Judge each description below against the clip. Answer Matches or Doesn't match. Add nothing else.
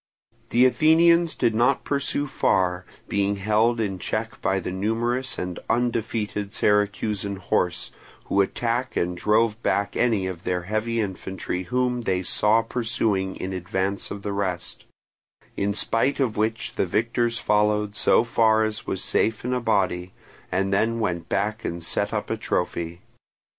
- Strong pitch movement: Doesn't match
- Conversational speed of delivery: Matches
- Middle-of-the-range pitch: Doesn't match